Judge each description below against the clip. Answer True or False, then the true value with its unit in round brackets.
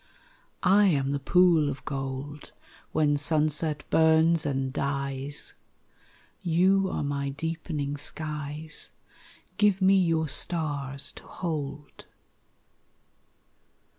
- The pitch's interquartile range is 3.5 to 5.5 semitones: False (2.8 semitones)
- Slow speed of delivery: True (95 wpm)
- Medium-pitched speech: True (150 Hz)